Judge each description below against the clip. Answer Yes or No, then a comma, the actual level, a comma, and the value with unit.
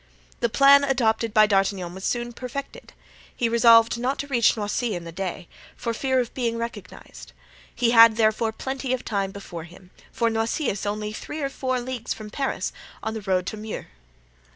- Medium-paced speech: Yes, average, 185 wpm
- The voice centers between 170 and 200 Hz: No, high, 230 Hz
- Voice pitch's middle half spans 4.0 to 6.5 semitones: No, average, 3.2 semitones